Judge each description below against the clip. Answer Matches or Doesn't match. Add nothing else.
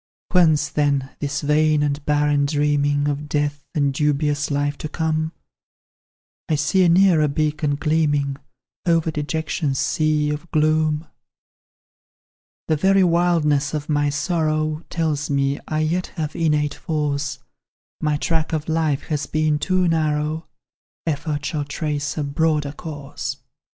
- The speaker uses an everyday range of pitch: Doesn't match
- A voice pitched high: Doesn't match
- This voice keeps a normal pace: Doesn't match